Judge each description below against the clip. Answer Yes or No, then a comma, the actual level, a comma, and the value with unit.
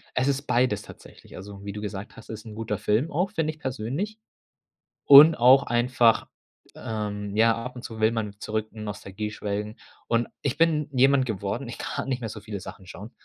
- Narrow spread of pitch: No, average, 3.9 semitones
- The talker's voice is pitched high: No, low, 115 Hz